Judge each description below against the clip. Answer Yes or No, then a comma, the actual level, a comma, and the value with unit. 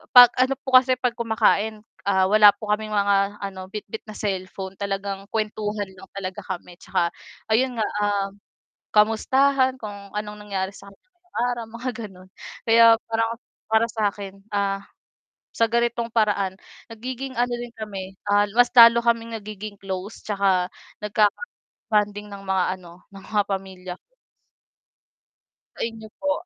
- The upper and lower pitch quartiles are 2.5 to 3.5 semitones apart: Yes, average, 2.8 semitones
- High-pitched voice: Yes, high, 210 Hz